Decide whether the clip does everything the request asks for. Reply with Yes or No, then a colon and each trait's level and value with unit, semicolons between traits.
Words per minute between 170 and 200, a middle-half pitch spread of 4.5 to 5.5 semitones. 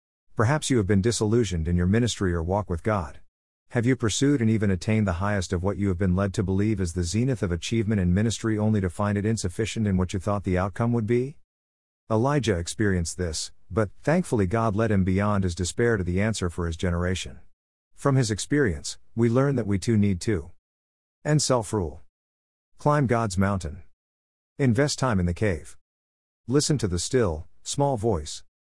Yes: average, 190 wpm; average, 4.9 semitones